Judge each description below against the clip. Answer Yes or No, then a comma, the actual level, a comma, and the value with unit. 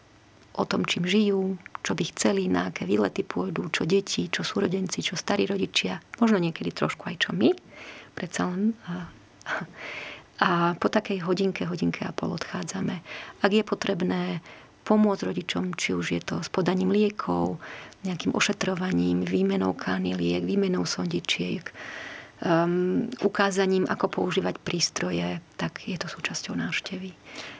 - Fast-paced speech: No, average, 135 wpm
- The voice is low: No, medium, 180 Hz